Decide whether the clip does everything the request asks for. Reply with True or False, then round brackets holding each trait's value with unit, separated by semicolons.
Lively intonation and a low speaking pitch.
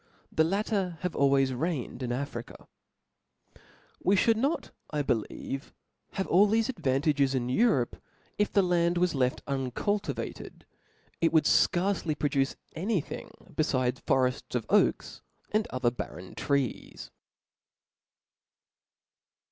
False (6.3 semitones; 150 Hz)